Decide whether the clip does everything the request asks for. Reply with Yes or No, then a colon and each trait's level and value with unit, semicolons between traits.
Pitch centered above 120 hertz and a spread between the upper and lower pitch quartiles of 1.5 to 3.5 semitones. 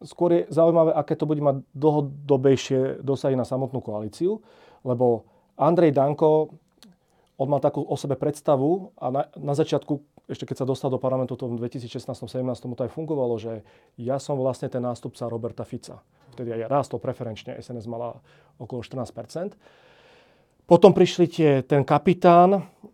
No: low, 135 Hz; average, 4.0 semitones